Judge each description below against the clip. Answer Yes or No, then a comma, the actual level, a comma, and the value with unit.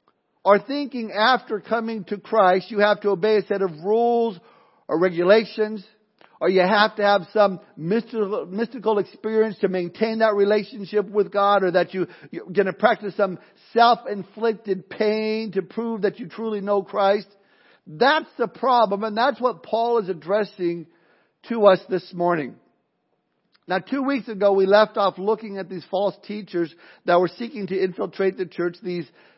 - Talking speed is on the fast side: No, average, 165 wpm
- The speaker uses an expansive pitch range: No, average, 2.7 semitones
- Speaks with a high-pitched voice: Yes, high, 205 Hz